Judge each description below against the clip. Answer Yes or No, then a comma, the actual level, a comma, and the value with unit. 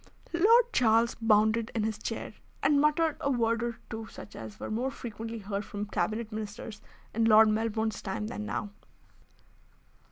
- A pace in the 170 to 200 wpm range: No, average, 160 wpm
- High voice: Yes, high, 225 Hz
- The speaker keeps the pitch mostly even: Yes, narrow, 1.8 semitones